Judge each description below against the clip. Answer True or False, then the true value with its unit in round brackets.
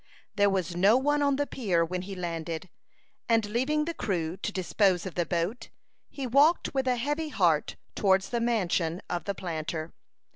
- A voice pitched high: True (195 Hz)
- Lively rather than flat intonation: True (6.4 semitones)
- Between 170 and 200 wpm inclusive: True (180 wpm)